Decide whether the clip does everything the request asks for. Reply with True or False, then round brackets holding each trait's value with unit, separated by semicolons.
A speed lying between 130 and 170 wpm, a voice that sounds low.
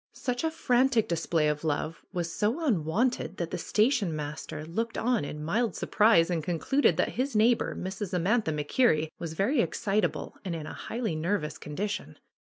False (165 wpm; 195 Hz)